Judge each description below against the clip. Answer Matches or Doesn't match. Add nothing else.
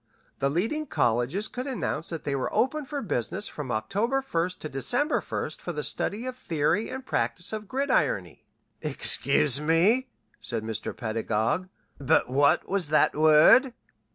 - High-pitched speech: Doesn't match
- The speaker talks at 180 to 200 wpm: Doesn't match